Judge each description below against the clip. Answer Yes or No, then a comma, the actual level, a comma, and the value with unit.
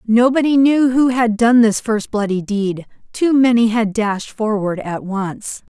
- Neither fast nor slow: Yes, average, 165 wpm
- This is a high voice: Yes, high, 225 Hz